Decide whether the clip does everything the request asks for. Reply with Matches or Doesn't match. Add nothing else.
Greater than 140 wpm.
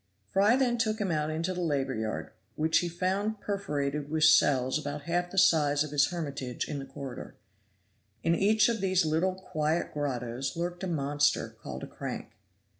Matches